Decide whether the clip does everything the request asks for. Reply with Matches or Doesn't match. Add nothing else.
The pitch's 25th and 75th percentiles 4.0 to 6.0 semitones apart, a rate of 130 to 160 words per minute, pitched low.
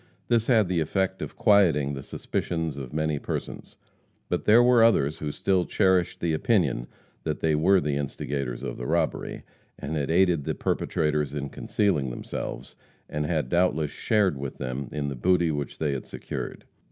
Doesn't match